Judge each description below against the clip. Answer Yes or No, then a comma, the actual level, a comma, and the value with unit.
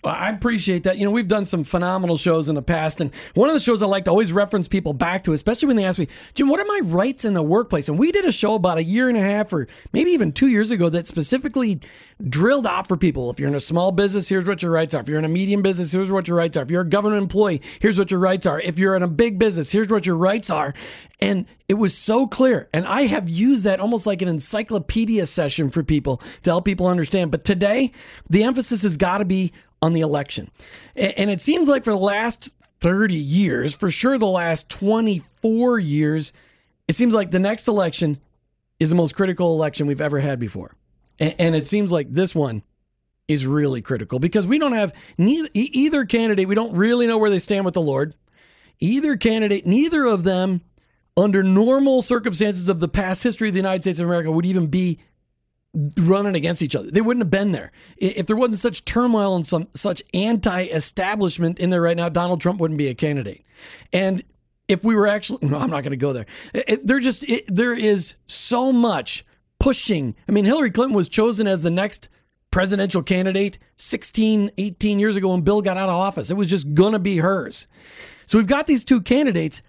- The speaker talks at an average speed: No, fast, 225 wpm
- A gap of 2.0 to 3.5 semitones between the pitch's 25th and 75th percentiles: No, average, 4.5 semitones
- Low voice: No, high, 190 Hz